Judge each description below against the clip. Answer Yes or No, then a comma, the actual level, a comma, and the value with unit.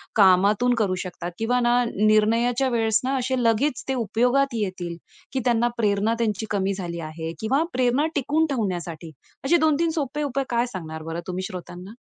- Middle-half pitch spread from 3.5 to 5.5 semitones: Yes, average, 5.2 semitones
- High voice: Yes, high, 225 Hz